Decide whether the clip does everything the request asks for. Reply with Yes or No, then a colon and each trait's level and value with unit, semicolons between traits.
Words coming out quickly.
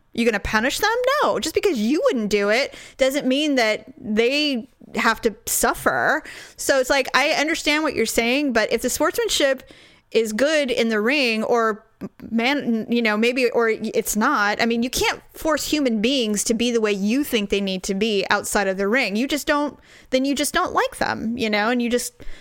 Yes: fast, 210 wpm